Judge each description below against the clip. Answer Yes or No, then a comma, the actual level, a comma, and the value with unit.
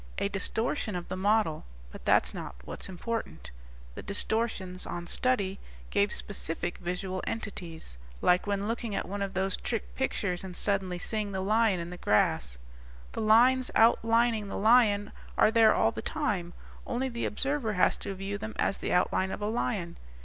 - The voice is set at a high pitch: Yes, high, 200 Hz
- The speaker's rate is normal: Yes, average, 170 wpm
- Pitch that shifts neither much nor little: Yes, average, 3.6 semitones